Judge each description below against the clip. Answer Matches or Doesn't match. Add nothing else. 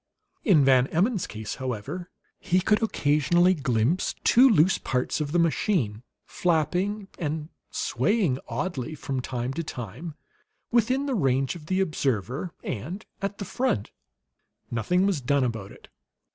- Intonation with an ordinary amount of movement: Doesn't match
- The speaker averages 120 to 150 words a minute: Matches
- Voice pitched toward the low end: Doesn't match